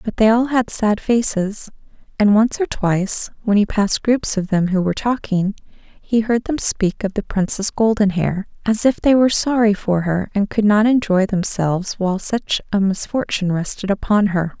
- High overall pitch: Yes, high, 210 Hz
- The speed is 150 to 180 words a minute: No, average, 190 wpm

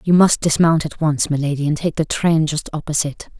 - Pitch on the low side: No, medium, 155 Hz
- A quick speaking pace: Yes, fast, 210 wpm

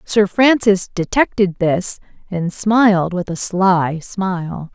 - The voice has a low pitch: No, high, 190 Hz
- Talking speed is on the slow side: Yes, slow, 125 wpm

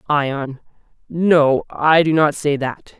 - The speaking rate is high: No, average, 140 wpm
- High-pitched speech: No, medium, 150 Hz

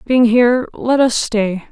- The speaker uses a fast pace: No, average, 175 wpm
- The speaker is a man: No, female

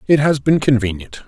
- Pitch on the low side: Yes, low, 130 Hz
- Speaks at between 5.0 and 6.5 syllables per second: Yes, 5.5 syllables/s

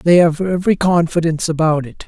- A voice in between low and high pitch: Yes, medium, 165 Hz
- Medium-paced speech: Yes, average, 145 wpm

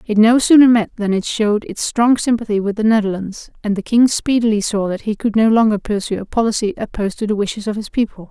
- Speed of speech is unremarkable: No, fast, 240 wpm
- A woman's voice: Yes, female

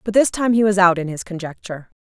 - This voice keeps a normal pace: No, fast, 265 wpm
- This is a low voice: No, high, 195 Hz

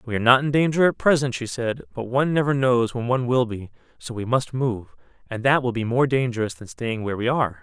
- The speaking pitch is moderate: No, low, 120 Hz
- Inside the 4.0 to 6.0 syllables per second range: No, 6.2 syllables/s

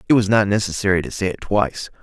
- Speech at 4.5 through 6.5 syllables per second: No, 7.0 syllables/s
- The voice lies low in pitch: Yes, low, 100 Hz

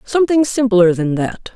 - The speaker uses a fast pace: No, average, 155 wpm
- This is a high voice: Yes, high, 220 Hz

